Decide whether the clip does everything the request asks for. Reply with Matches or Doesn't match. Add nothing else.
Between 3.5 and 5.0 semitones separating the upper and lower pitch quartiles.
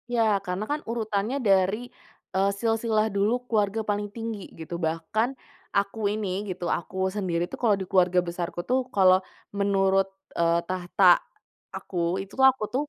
Doesn't match